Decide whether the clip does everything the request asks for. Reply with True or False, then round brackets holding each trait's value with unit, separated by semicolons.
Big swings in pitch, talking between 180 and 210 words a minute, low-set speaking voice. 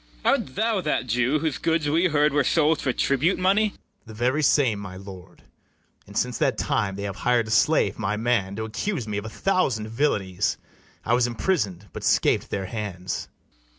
True (6.7 semitones; 200 wpm; 120 Hz)